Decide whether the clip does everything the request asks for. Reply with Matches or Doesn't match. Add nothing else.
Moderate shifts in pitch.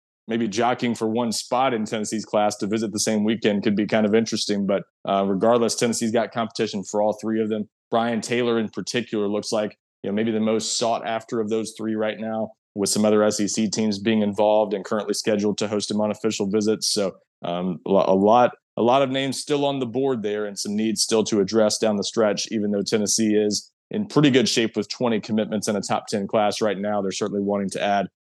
Doesn't match